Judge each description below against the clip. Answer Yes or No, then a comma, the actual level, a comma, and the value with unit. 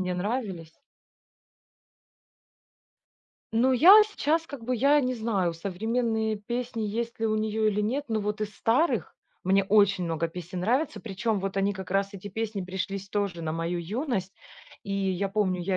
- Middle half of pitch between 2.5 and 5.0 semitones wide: Yes, average, 3.5 semitones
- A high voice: Yes, high, 205 Hz